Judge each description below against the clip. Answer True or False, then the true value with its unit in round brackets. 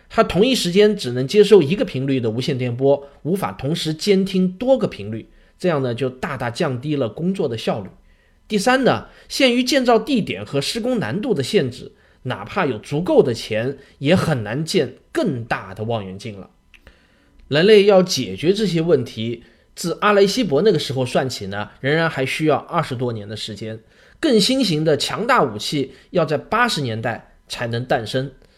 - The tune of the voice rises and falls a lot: True (8.4 semitones)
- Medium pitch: True (150 Hz)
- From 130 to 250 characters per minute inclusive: False (270 characters per minute)